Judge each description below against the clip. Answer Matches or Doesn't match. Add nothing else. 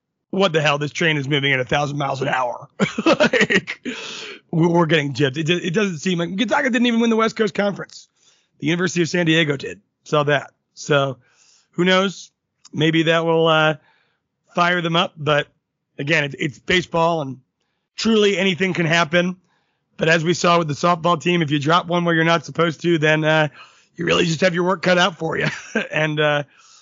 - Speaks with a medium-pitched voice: Matches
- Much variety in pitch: Doesn't match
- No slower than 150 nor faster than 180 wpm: Doesn't match